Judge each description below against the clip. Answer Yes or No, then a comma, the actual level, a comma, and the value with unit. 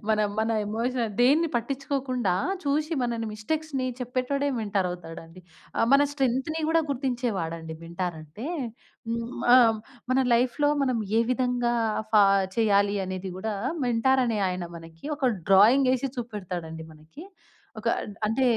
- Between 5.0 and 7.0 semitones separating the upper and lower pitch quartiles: Yes, wide, 5.4 semitones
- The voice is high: Yes, high, 235 Hz